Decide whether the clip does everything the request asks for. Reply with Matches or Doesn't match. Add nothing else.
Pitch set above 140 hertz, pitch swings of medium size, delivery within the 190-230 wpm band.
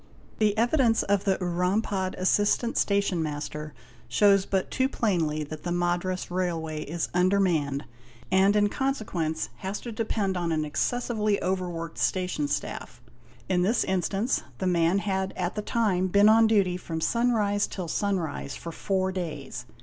Doesn't match